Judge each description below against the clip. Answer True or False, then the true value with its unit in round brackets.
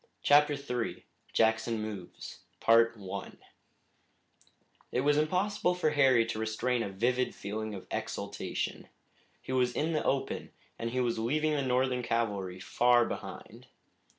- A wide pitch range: False (4.1 semitones)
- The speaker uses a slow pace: True (125 wpm)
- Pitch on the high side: False (125 Hz)